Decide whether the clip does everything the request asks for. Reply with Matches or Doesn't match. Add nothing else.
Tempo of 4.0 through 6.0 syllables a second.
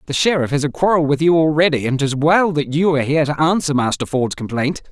Doesn't match